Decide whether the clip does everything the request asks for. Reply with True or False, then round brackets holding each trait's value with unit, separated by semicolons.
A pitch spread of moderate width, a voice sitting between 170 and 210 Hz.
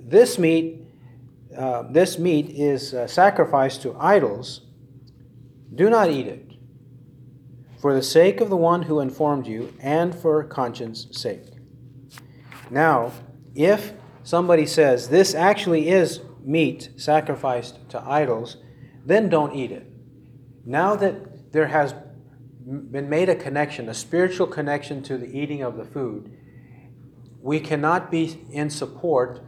False (3.8 semitones; 135 Hz)